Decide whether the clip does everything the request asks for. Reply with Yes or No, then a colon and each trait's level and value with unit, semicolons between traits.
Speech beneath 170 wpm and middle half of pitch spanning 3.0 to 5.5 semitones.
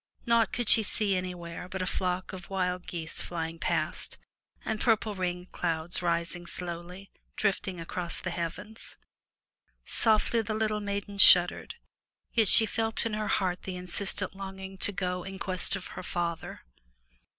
No: average, 150 wpm; narrow, 2.6 semitones